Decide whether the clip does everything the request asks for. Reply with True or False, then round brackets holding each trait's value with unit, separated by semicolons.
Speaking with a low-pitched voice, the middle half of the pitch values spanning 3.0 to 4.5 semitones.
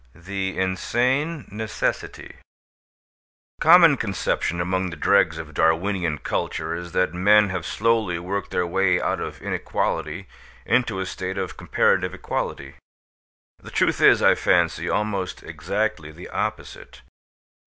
True (95 Hz; 3.4 semitones)